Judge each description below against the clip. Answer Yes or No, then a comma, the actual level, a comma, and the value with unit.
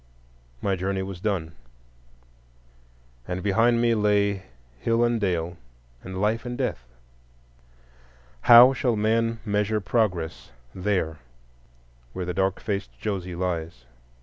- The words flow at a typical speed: No, slow, 115 wpm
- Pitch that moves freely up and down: No, average, 3.9 semitones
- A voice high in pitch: No, low, 100 Hz